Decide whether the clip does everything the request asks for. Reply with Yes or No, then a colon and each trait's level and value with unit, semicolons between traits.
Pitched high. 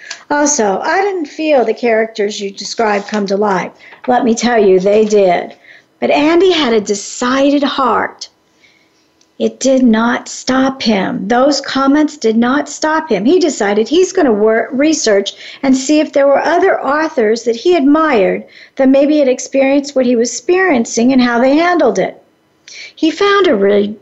Yes: very high, 260 Hz